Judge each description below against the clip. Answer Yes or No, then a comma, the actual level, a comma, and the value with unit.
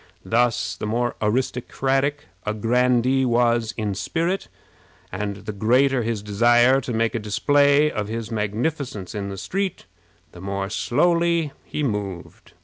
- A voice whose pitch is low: Yes, low, 120 Hz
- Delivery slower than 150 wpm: Yes, average, 140 wpm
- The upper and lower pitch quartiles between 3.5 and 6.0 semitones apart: Yes, average, 4.3 semitones